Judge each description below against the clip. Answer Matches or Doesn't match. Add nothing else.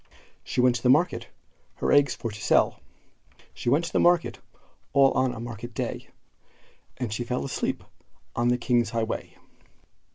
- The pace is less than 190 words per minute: Matches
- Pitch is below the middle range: Matches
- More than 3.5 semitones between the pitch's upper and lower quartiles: Doesn't match